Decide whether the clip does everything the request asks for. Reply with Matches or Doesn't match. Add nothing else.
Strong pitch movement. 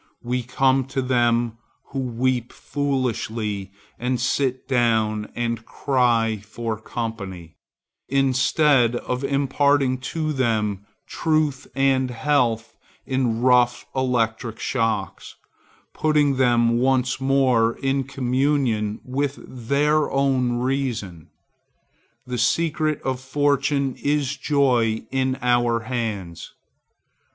Doesn't match